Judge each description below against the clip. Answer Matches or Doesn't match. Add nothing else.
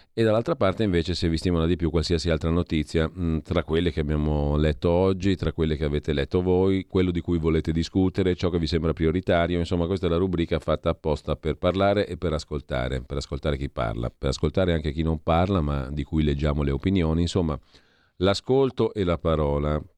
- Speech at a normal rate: Doesn't match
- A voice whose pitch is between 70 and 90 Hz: Matches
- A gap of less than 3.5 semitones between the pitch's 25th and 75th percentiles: Matches